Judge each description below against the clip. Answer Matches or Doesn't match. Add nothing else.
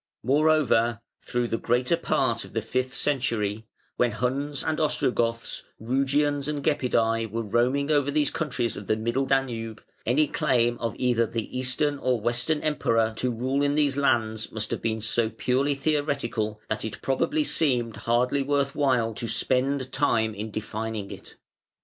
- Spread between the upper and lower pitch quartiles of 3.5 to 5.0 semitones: Matches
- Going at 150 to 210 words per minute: Matches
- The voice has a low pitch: Matches